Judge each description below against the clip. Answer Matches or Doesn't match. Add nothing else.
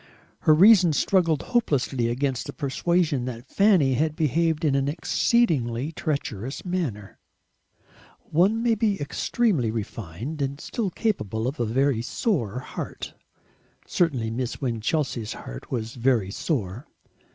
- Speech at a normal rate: Doesn't match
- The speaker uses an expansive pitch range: Matches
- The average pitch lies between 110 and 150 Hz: Matches